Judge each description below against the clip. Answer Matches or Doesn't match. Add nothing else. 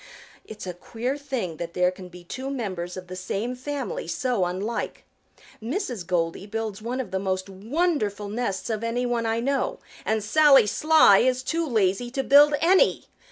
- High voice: Matches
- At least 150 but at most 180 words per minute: Matches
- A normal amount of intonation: Doesn't match